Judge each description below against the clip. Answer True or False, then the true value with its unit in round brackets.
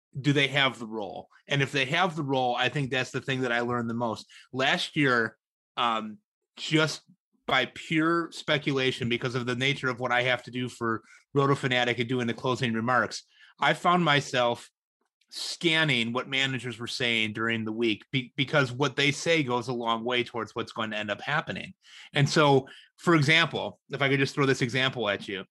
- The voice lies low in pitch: True (130 Hz)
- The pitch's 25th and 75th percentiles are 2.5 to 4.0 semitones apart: True (3.1 semitones)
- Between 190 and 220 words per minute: True (200 wpm)